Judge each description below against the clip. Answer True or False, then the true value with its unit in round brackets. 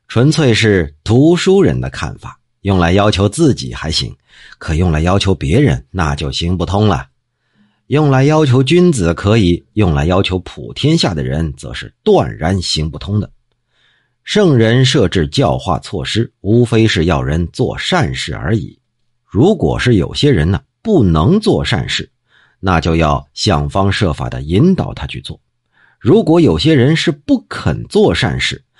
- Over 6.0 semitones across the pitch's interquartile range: True (7.6 semitones)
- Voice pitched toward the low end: True (105 Hz)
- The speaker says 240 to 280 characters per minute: False (225 characters per minute)